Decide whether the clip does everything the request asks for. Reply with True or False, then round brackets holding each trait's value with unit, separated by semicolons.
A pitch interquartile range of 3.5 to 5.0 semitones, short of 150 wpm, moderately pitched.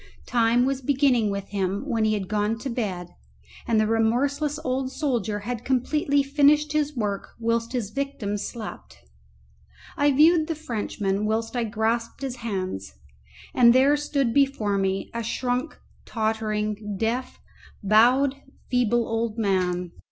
False (4.3 semitones; 140 wpm; 230 Hz)